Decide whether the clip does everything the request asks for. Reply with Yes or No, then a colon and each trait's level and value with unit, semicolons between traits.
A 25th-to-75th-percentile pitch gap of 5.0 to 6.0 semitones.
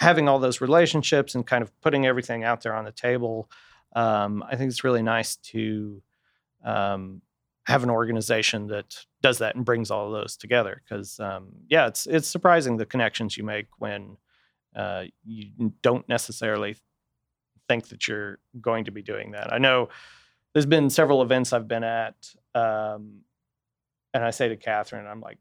No: average, 3.3 semitones